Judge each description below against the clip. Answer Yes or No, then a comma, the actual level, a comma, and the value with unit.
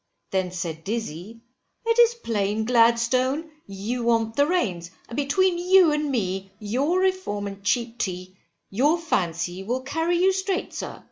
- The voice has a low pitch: No, high, 235 Hz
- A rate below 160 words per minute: Yes, average, 150 wpm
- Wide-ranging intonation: Yes, wide, 8.7 semitones